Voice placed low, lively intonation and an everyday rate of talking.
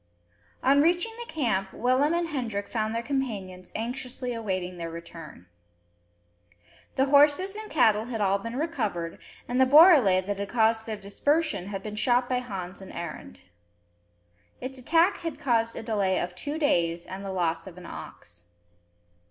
No: high, 225 Hz; wide, 6.4 semitones; average, 160 wpm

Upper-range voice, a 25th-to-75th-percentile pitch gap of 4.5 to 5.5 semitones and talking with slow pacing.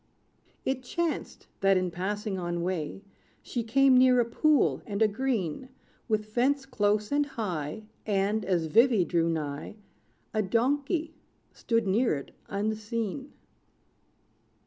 Yes: high, 215 Hz; average, 5.2 semitones; slow, 125 wpm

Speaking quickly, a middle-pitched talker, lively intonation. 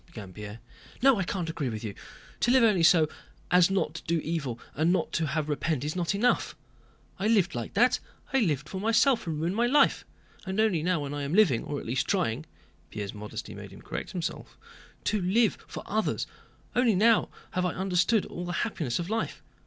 Yes: fast, 210 wpm; medium, 175 Hz; wide, 6.2 semitones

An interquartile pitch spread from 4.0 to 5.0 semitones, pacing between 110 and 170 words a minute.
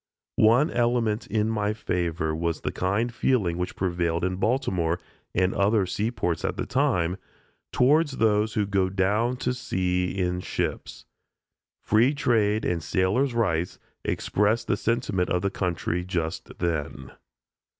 Yes: average, 4.5 semitones; average, 140 wpm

